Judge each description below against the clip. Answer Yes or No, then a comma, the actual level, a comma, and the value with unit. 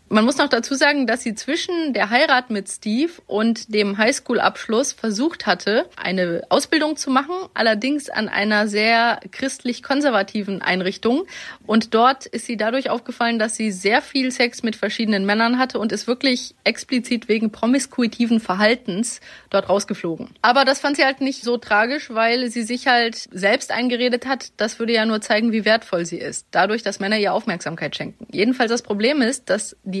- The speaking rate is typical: Yes, average, 175 wpm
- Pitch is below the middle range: No, high, 230 Hz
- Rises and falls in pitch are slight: No, average, 3.4 semitones